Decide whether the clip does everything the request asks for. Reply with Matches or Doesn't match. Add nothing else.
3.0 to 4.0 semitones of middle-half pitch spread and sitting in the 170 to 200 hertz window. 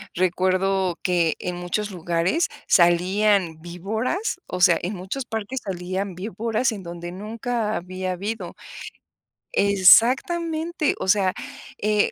Matches